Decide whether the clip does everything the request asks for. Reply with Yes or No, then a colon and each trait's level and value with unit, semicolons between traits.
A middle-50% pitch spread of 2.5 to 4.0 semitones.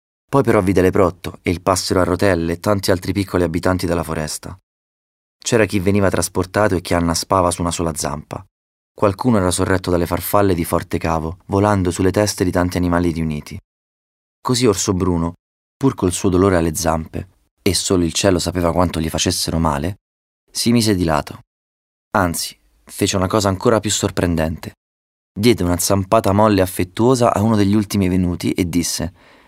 Yes: average, 3.3 semitones